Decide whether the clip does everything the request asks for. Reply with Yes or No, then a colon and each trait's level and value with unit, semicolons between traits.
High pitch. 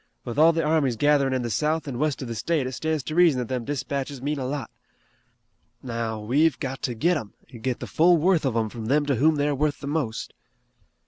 No: medium, 140 Hz